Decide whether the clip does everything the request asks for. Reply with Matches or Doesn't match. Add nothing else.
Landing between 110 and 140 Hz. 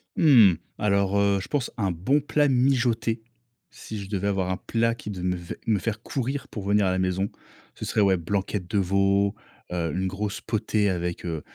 Doesn't match